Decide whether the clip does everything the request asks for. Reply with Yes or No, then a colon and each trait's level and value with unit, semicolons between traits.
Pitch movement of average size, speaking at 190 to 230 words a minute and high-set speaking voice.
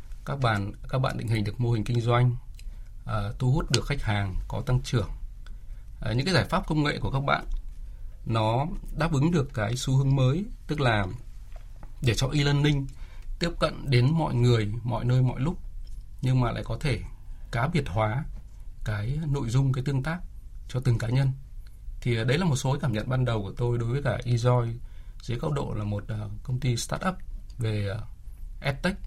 No: average, 4.3 semitones; average, 200 wpm; low, 120 Hz